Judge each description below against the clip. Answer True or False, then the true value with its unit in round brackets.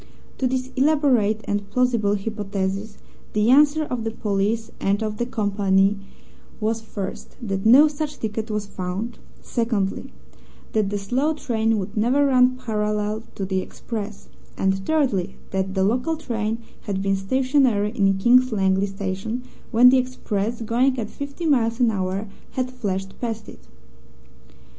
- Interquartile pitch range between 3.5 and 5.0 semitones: True (4.1 semitones)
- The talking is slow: False (150 wpm)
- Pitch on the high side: True (220 Hz)